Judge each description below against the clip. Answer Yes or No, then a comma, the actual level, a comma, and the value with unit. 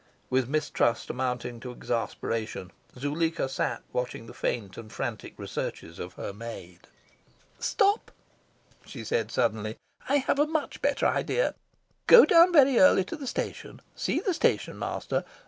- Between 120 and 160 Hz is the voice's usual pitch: Yes, low, 135 Hz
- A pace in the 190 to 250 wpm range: No, average, 145 wpm